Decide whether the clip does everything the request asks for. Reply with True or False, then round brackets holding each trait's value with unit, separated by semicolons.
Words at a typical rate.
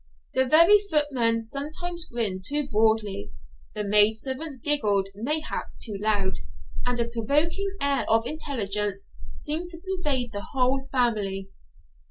False (125 wpm)